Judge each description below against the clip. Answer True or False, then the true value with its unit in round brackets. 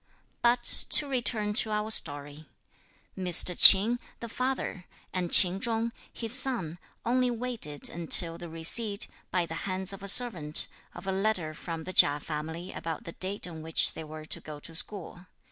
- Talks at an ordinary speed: True (170 wpm)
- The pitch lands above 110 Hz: True (185 Hz)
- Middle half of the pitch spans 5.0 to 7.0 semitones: True (5.5 semitones)